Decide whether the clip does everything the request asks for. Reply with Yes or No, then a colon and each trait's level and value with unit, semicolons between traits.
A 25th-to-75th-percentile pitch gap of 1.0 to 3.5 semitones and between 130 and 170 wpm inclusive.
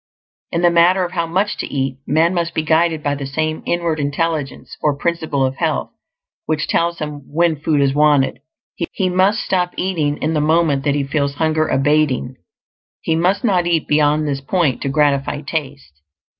No: average, 3.0 semitones; average, 185 wpm